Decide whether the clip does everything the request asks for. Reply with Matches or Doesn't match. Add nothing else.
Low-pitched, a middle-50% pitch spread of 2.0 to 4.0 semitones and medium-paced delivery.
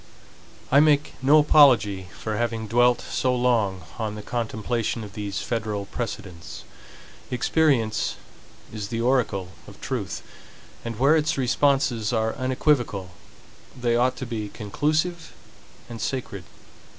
Doesn't match